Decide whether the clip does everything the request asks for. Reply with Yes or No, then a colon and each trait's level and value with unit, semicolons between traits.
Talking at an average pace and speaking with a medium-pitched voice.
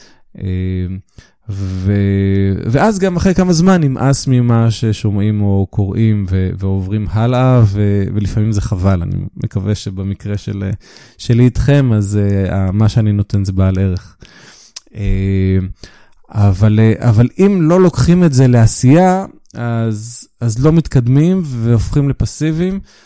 No: average, 115 wpm; low, 110 Hz